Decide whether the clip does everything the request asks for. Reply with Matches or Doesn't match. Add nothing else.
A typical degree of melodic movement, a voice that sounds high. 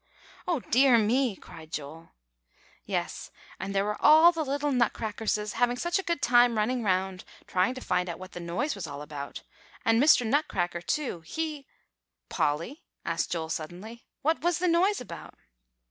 Doesn't match